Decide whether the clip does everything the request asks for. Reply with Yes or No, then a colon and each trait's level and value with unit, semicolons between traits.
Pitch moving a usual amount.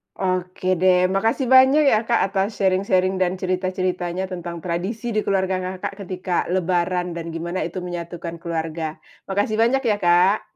No: narrow, 1.9 semitones